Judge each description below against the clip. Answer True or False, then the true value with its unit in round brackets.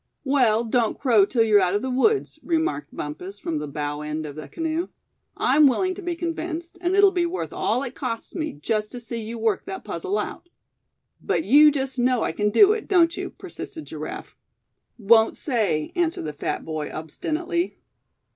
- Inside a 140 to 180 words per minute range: False (190 wpm)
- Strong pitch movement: True (8.7 semitones)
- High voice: True (245 Hz)